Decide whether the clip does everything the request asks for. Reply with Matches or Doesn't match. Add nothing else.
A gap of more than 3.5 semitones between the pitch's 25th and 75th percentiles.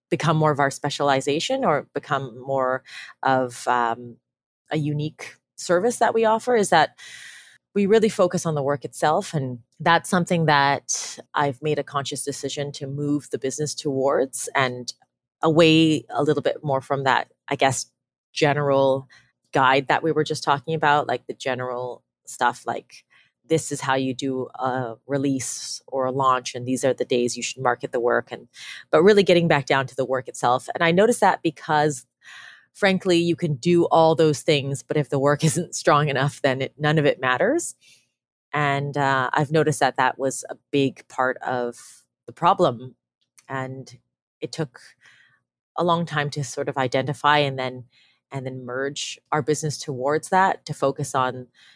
Doesn't match